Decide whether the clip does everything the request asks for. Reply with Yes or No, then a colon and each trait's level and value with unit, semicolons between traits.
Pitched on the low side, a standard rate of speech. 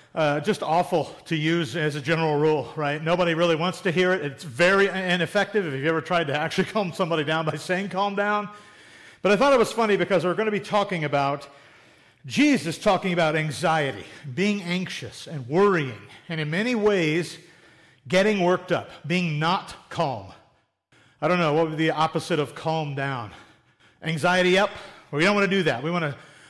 No: medium, 165 Hz; average, 190 wpm